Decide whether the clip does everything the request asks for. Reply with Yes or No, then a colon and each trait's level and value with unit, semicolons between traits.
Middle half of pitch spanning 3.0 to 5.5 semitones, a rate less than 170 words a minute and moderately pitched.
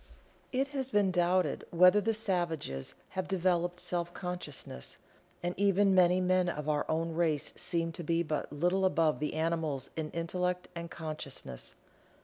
No: narrow, 2.4 semitones; average, 150 wpm; medium, 175 Hz